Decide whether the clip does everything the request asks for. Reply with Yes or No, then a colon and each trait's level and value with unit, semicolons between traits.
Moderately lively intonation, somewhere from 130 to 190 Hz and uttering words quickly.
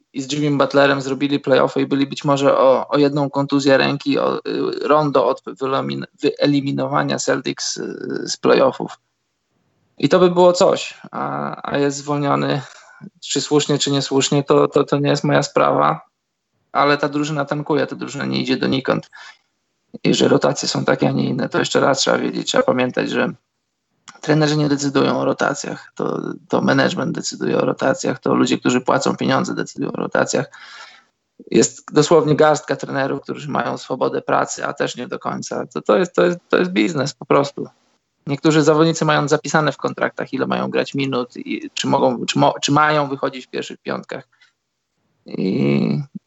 Yes: average, 3.5 semitones; medium, 140 Hz; fast, 175 wpm